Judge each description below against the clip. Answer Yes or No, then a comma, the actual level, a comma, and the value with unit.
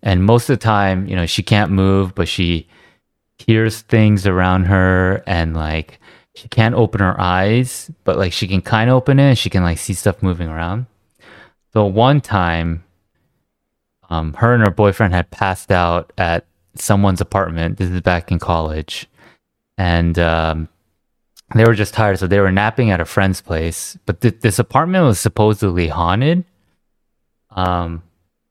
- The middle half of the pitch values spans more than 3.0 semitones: Yes, average, 4.4 semitones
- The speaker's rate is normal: Yes, average, 170 wpm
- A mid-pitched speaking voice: No, very low, 95 Hz